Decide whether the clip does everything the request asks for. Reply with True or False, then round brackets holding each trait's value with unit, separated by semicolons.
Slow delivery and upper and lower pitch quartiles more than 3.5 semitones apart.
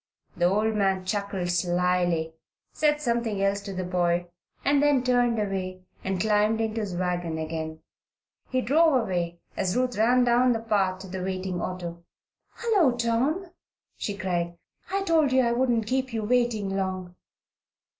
False (155 wpm; 5.2 semitones)